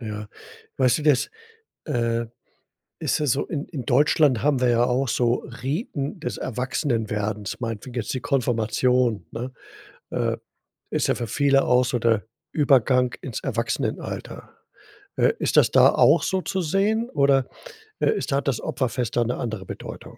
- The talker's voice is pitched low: Yes, low, 125 Hz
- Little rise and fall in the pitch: No, average, 3.3 semitones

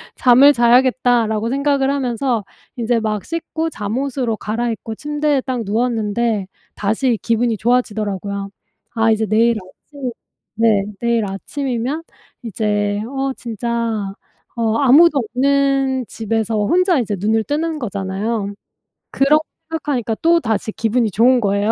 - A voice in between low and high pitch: No, high, 235 Hz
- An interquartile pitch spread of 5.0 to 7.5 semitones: No, average, 3.8 semitones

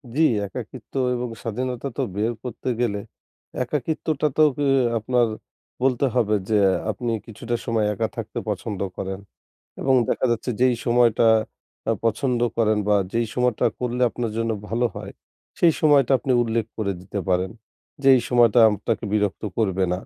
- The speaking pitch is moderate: No, low, 120 Hz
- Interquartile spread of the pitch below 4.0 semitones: Yes, average, 2.8 semitones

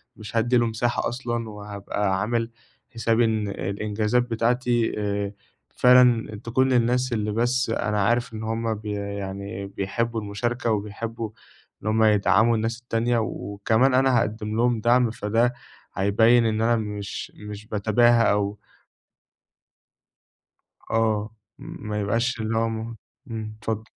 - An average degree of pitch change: No, narrow, 2.1 semitones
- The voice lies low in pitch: Yes, low, 110 Hz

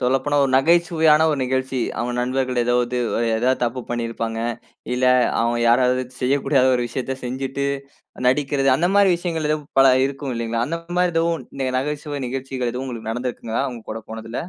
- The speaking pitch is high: No, low, 130 Hz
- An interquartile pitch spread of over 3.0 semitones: No, average, 2.7 semitones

